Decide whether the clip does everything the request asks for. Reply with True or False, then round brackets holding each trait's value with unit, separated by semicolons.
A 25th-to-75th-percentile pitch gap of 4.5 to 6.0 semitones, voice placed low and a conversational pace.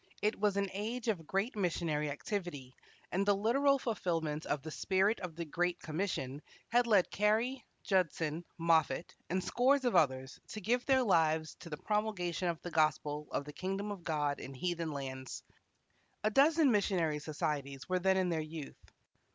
False (5.3 semitones; 175 Hz; 170 wpm)